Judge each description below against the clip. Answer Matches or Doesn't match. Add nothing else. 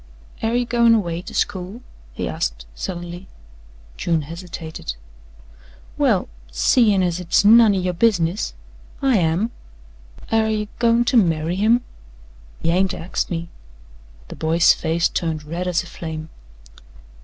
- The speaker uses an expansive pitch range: Doesn't match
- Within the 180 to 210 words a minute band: Doesn't match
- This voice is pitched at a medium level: Matches